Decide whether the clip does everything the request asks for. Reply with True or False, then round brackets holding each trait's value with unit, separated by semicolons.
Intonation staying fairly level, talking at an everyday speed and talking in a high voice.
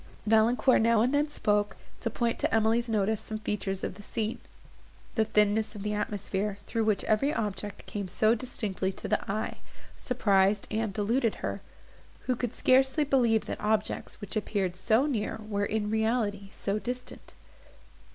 True (2.1 semitones; 160 wpm; 215 Hz)